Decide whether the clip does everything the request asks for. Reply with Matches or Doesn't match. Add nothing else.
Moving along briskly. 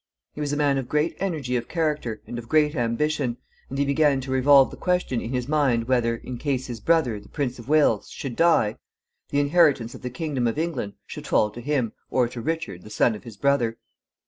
Matches